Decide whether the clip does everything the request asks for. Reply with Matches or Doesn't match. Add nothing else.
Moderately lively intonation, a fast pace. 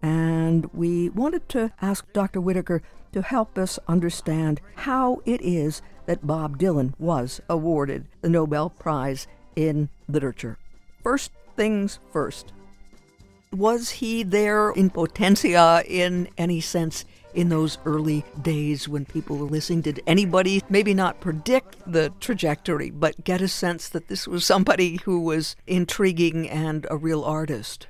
Doesn't match